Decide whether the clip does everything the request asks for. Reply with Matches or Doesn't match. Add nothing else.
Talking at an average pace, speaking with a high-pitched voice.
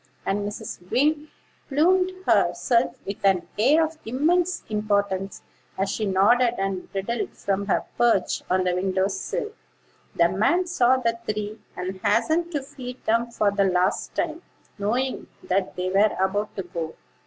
Matches